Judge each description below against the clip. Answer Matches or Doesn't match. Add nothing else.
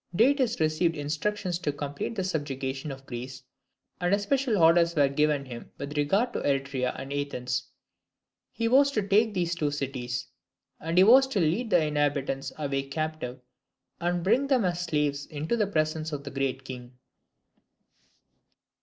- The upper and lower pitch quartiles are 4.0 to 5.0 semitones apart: Doesn't match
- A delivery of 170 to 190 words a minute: Doesn't match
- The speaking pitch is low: Doesn't match